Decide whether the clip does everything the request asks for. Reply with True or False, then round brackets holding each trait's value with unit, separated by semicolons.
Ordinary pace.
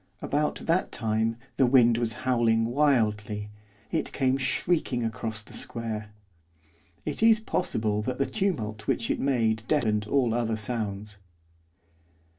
False (130 wpm)